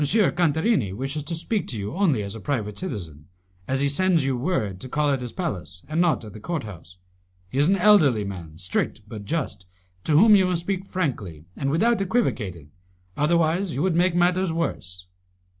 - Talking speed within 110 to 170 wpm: No, average, 190 wpm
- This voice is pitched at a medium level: Yes, medium, 145 Hz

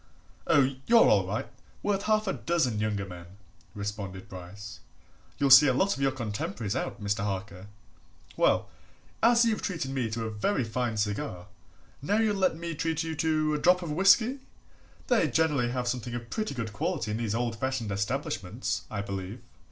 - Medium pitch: No, low, 125 Hz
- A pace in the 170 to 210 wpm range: Yes, average, 175 wpm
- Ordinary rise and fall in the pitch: No, wide, 7.8 semitones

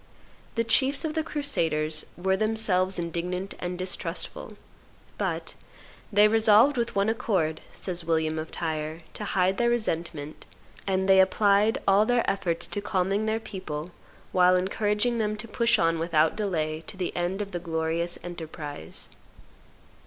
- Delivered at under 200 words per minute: Yes, average, 150 wpm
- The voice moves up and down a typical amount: Yes, average, 4.5 semitones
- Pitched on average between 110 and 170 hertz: No, high, 190 Hz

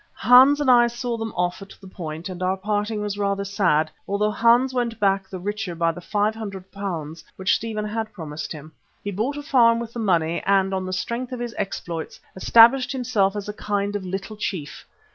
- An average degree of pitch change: Yes, average, 3.6 semitones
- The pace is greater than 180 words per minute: Yes, average, 200 wpm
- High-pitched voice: Yes, high, 205 Hz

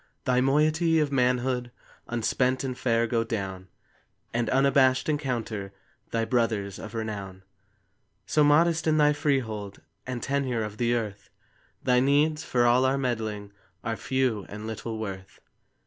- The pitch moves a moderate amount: Yes, average, 3.8 semitones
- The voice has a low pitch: Yes, low, 120 Hz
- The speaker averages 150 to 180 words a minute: No, average, 140 wpm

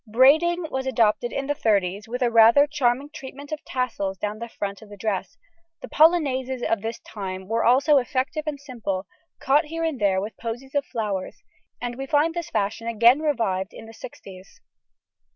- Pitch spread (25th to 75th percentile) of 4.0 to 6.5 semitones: Yes, average, 5.1 semitones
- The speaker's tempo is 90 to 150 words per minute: No, average, 185 wpm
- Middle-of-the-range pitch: No, high, 240 Hz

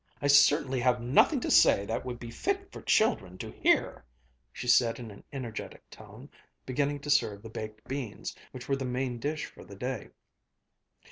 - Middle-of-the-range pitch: No, low, 125 Hz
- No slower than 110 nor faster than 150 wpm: No, average, 185 wpm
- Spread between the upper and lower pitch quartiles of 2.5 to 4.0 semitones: Yes, average, 3.7 semitones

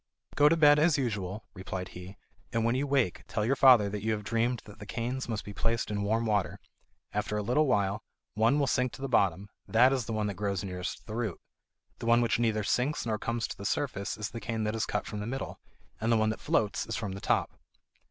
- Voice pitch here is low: Yes, low, 110 Hz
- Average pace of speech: No, fast, 245 wpm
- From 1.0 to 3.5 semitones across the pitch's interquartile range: Yes, average, 3.1 semitones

